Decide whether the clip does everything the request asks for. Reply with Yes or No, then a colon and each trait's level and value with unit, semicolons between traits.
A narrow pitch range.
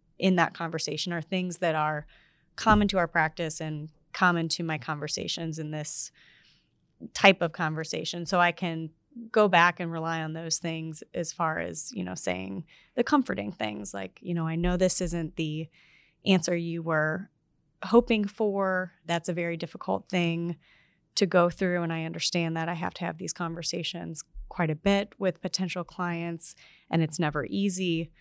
Yes: narrow, 2.2 semitones